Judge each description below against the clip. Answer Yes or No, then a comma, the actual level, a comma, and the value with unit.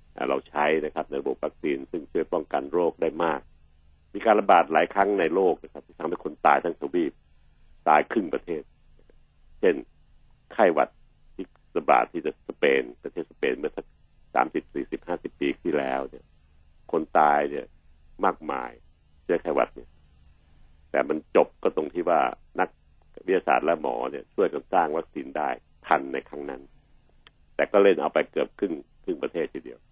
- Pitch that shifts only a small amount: Yes, narrow, 1.2 semitones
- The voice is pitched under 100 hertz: Yes, very low, 75 Hz